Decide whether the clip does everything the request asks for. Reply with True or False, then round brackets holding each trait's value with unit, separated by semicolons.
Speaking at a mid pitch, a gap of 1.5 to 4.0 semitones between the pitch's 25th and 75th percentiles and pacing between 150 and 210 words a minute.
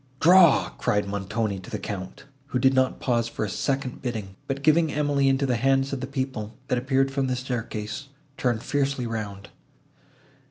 False (130 Hz; 3.7 semitones; 175 wpm)